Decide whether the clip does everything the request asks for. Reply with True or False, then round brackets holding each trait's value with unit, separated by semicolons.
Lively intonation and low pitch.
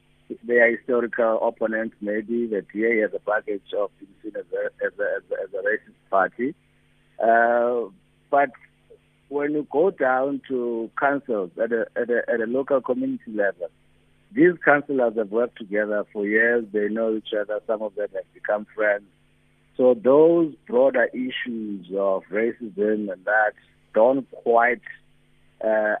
True (7.1 semitones; 120 Hz)